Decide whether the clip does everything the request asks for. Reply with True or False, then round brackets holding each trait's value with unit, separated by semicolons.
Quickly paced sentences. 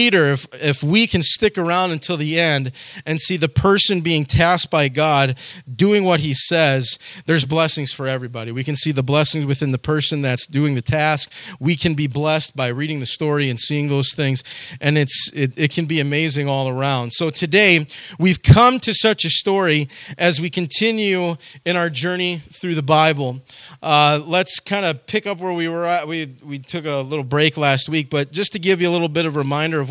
True (210 wpm)